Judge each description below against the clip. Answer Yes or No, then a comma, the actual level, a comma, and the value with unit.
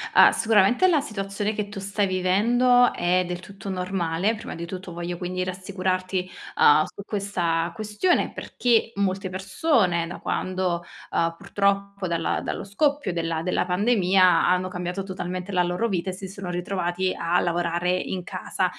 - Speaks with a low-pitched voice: No, medium, 185 Hz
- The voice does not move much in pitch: Yes, narrow, 2.1 semitones